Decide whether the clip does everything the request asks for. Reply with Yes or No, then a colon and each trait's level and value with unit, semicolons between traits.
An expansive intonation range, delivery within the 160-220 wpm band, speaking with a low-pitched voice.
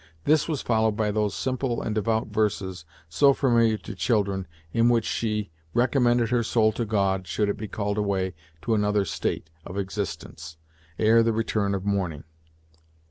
No: average, 2.7 semitones; average, 165 wpm; low, 105 Hz